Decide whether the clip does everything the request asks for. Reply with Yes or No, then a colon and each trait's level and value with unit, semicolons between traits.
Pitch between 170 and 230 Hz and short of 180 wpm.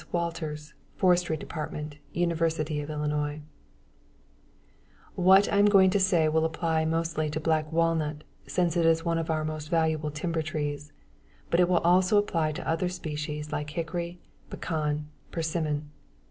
No: medium, 160 Hz; average, 145 wpm